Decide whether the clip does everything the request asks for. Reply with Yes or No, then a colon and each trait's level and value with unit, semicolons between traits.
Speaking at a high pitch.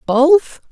Yes: very high, 300 Hz